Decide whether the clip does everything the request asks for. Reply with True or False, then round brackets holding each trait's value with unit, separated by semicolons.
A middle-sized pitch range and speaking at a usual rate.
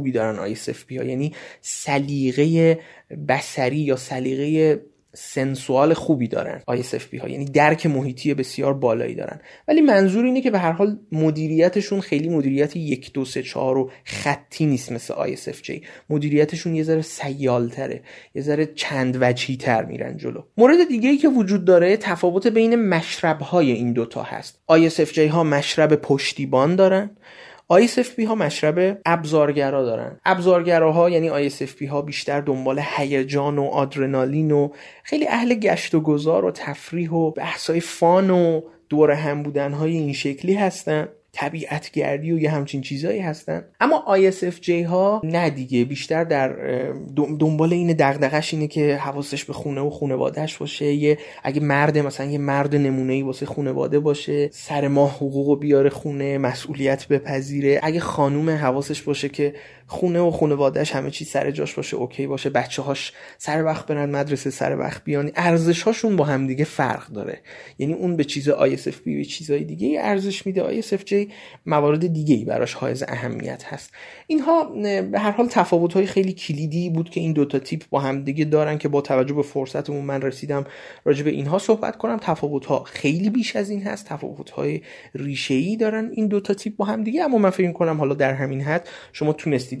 False (3.7 semitones; 170 wpm)